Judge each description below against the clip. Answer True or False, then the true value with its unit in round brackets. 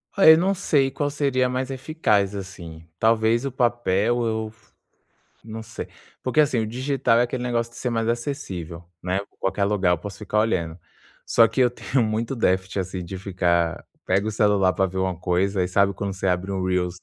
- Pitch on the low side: True (110 Hz)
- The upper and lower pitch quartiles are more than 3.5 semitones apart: True (4.6 semitones)